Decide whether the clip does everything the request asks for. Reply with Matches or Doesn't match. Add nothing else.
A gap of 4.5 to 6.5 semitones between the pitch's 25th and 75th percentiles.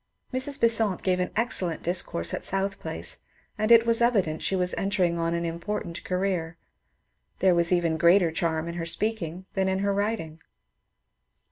Doesn't match